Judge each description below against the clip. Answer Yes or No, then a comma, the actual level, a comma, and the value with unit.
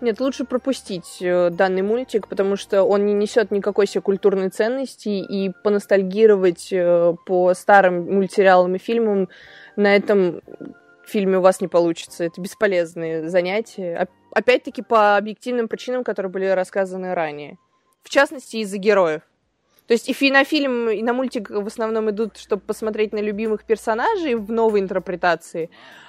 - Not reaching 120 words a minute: No, average, 145 wpm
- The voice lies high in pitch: Yes, high, 205 Hz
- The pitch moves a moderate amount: Yes, average, 3.3 semitones